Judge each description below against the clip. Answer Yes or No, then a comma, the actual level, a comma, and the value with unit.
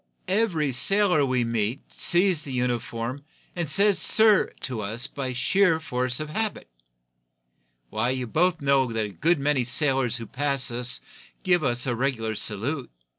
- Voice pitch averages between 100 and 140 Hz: Yes, low, 135 Hz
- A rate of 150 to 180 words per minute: Yes, average, 155 wpm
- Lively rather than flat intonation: No, average, 4.7 semitones